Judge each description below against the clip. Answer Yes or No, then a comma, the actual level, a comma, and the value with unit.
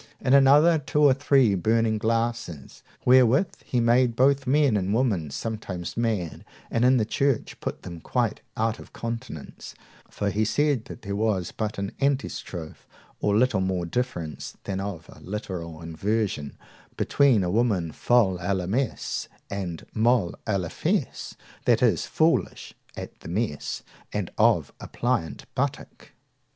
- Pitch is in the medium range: No, low, 110 Hz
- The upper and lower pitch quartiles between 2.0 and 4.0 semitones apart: No, average, 5.3 semitones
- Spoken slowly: No, average, 150 wpm